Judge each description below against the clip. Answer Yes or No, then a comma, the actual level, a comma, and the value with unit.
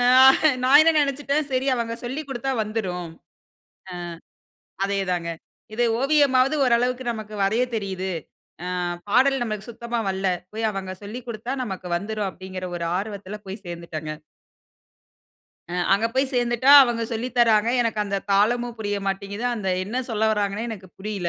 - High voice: Yes, high, 220 Hz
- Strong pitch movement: No, average, 3.9 semitones